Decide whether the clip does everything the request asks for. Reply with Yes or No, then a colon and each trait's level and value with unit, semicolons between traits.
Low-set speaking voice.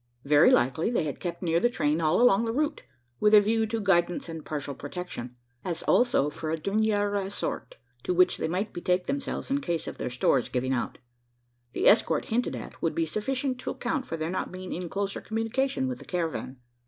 No: high, 190 Hz